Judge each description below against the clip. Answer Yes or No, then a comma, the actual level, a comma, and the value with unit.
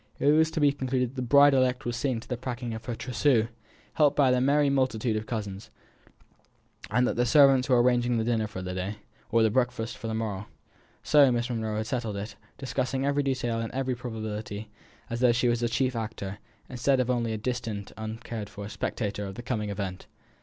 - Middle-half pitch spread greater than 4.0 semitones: No, average, 2.8 semitones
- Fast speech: Yes, fast, 210 wpm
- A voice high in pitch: No, low, 120 Hz